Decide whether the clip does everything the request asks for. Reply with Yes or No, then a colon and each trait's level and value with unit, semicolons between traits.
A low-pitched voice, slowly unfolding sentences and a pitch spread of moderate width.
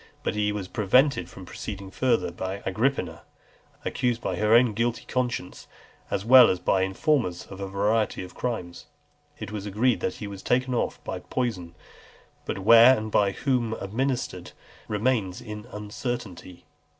No: low, 105 Hz; average, 155 wpm; average, 4.2 semitones